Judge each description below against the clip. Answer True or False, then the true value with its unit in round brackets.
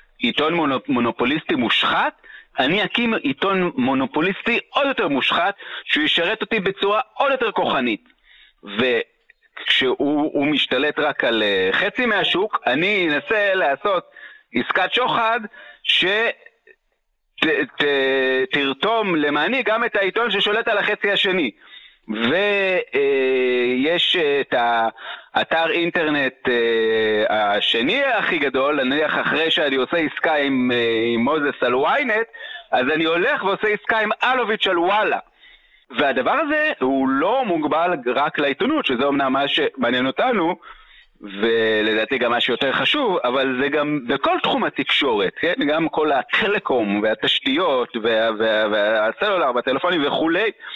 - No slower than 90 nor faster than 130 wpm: True (120 wpm)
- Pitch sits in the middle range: True (165 Hz)